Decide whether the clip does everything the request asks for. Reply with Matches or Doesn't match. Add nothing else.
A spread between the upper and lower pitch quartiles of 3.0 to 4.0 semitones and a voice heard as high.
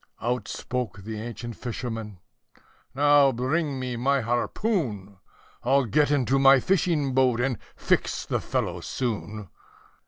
Doesn't match